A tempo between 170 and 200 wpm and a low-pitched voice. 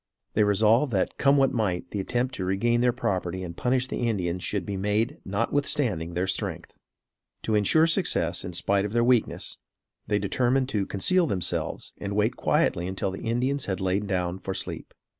Yes: average, 180 wpm; low, 105 Hz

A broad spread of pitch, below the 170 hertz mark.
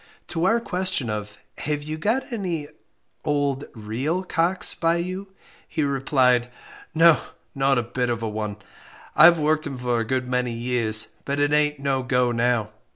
No: average, 5.0 semitones; medium, 140 Hz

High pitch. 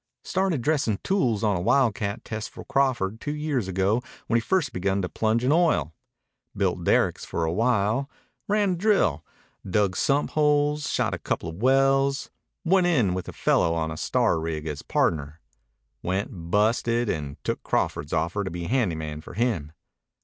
No: low, 110 Hz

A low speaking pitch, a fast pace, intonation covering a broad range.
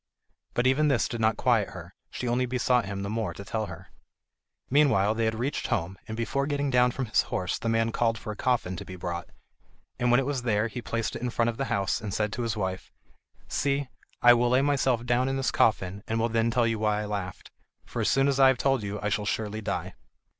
No: low, 115 Hz; fast, 245 wpm; average, 3.2 semitones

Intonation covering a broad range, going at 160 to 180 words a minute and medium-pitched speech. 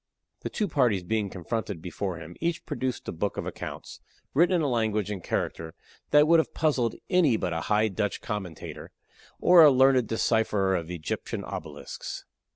No: wide, 6.6 semitones; average, 170 wpm; low, 110 Hz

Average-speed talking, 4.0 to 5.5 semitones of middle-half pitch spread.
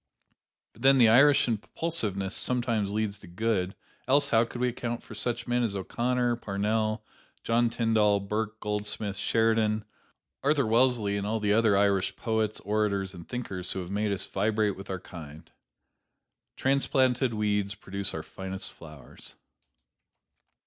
No: average, 145 wpm; average, 3.0 semitones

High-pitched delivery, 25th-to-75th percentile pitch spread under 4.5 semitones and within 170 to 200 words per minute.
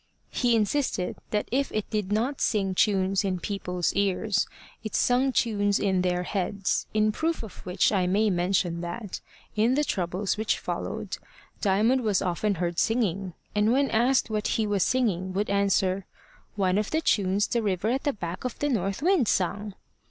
Yes: high, 205 Hz; average, 3.3 semitones; average, 175 wpm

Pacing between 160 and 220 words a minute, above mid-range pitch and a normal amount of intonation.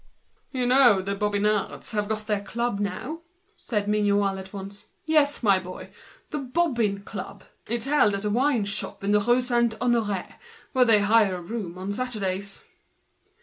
Yes: average, 170 wpm; high, 210 Hz; average, 3.3 semitones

